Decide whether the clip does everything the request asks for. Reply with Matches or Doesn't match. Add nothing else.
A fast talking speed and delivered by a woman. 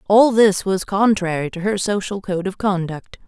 Doesn't match